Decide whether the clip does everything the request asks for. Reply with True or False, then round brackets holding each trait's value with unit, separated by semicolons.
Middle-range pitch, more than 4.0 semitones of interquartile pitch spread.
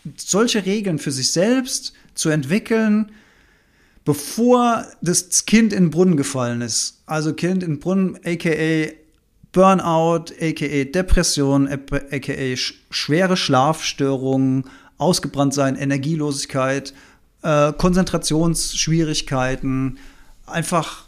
True (155 Hz; 4.8 semitones)